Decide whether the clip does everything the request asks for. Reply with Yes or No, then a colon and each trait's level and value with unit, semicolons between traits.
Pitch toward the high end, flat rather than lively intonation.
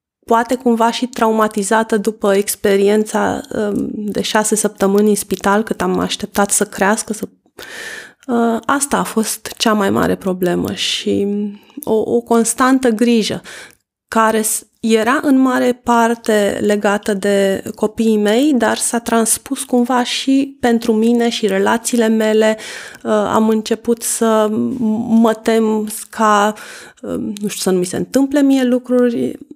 Yes: high, 225 Hz; narrow, 2.1 semitones